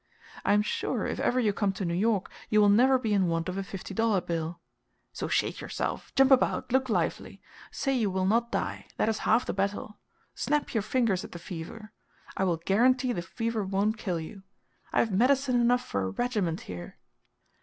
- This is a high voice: Yes, high, 210 Hz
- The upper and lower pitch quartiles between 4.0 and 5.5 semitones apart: Yes, average, 4.5 semitones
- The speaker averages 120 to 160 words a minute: No, fast, 205 wpm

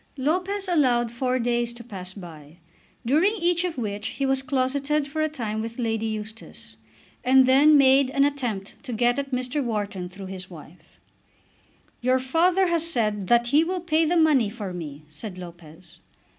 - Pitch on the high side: Yes, high, 245 Hz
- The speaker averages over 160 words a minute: Yes, average, 170 wpm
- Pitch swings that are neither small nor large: No, wide, 5.9 semitones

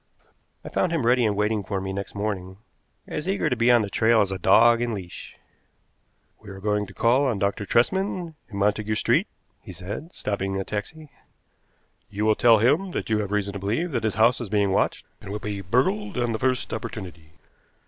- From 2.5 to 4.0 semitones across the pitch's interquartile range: Yes, average, 3.4 semitones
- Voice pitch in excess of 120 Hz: No, low, 110 Hz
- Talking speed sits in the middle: No, fast, 210 wpm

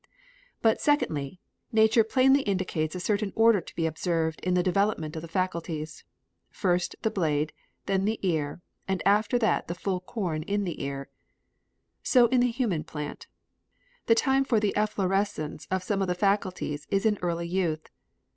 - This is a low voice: No, medium, 185 Hz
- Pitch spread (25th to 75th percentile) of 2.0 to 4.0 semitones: No, average, 4.7 semitones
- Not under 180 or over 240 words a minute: No, average, 165 wpm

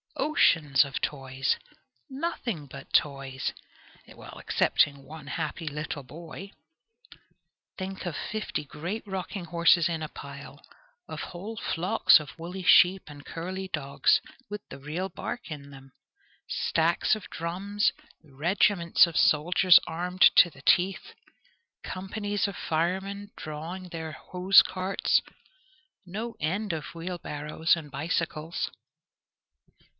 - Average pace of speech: No, slow, 120 wpm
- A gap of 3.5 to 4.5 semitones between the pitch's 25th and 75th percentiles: Yes, average, 4.1 semitones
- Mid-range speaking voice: Yes, medium, 170 Hz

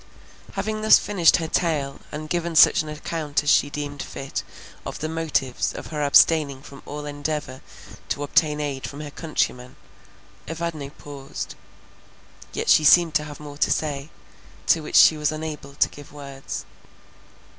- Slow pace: No, average, 160 wpm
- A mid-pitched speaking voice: Yes, medium, 150 Hz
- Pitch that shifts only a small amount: Yes, narrow, 1.9 semitones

